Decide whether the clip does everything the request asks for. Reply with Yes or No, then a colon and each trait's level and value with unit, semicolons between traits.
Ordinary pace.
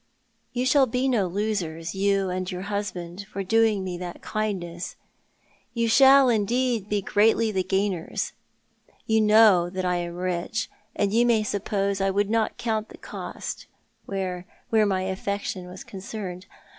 Yes: average, 155 wpm